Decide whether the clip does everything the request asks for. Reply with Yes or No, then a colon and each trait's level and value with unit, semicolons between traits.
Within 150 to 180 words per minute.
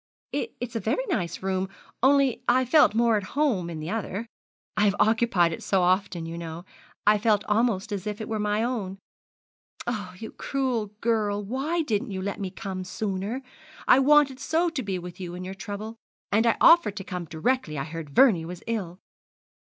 No: average, 190 wpm